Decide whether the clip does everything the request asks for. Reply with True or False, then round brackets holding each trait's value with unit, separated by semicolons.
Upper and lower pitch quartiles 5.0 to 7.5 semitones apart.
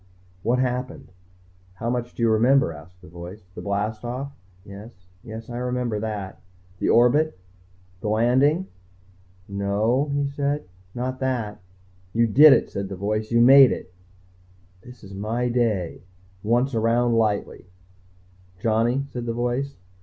False (3.2 semitones)